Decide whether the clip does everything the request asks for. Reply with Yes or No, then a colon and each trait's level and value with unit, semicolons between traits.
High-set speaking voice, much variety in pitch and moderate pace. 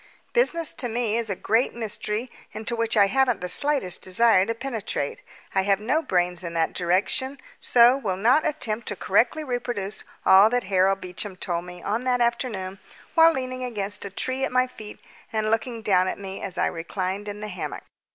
No: high, 215 Hz; average, 4.5 semitones; average, 190 wpm